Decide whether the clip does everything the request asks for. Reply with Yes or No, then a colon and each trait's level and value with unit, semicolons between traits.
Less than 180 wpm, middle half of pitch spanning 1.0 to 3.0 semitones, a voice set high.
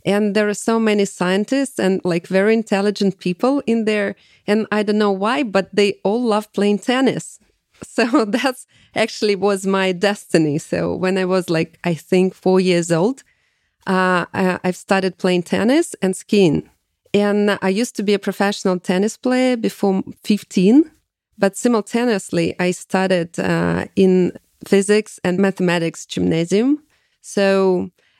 Yes: average, 150 wpm; narrow, 2.4 semitones; high, 195 Hz